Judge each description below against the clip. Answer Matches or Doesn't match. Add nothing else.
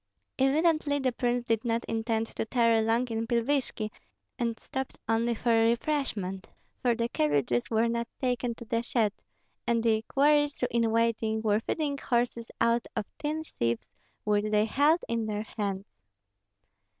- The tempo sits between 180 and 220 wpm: Doesn't match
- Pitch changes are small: Matches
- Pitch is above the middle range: Matches